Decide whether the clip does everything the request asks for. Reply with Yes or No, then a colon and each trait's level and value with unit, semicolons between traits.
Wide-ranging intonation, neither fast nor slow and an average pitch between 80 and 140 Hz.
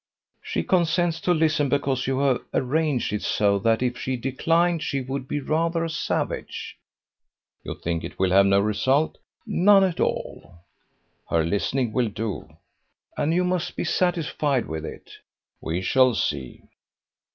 Yes: wide, 7.5 semitones; average, 150 wpm; low, 135 Hz